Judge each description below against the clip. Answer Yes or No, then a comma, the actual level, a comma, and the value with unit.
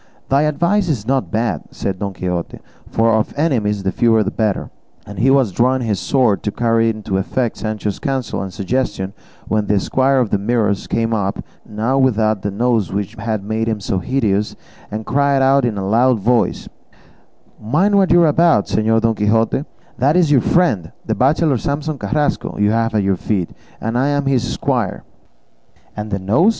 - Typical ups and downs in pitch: Yes, average, 4.4 semitones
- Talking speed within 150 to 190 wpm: Yes, average, 185 wpm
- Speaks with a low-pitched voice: Yes, low, 115 Hz